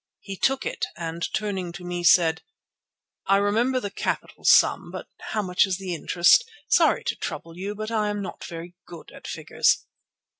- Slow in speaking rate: No, average, 180 wpm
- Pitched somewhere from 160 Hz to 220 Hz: Yes, high, 190 Hz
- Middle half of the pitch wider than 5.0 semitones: No, average, 3.2 semitones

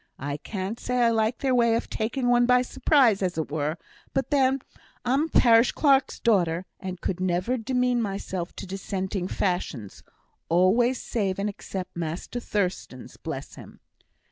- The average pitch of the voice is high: Yes, high, 210 Hz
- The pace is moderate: Yes, average, 160 wpm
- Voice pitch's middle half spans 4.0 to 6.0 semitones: Yes, average, 5.2 semitones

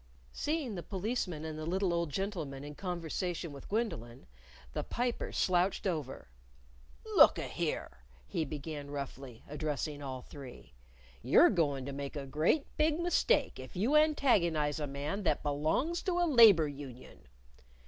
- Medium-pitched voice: Yes, medium, 160 Hz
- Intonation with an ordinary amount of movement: No, wide, 6.3 semitones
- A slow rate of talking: No, average, 150 wpm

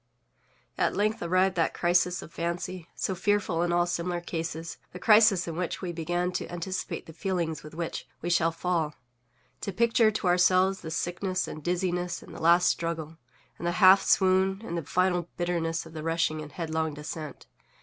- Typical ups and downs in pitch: No, narrow, 2.0 semitones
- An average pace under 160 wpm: No, average, 175 wpm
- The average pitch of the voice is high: No, medium, 175 Hz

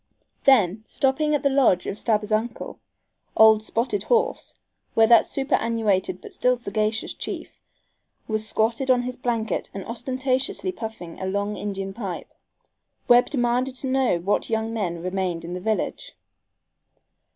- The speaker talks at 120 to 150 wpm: Yes, average, 140 wpm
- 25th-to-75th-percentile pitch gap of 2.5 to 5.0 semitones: Yes, average, 4.0 semitones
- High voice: Yes, high, 225 Hz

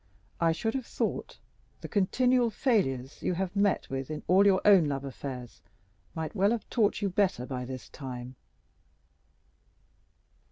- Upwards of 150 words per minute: No, average, 145 wpm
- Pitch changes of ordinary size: No, wide, 7.5 semitones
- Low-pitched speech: No, medium, 180 Hz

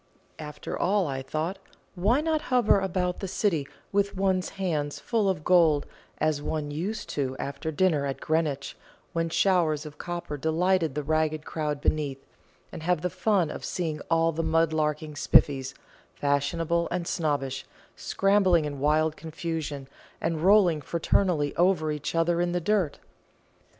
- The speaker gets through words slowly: No, average, 150 wpm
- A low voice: No, medium, 165 Hz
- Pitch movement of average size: Yes, average, 3.4 semitones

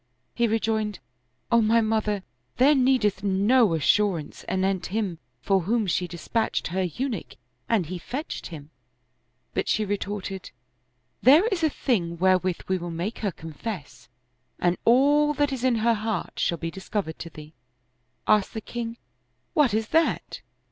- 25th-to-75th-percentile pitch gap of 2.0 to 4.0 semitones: No, average, 4.6 semitones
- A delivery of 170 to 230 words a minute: No, average, 155 wpm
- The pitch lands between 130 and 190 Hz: No, high, 210 Hz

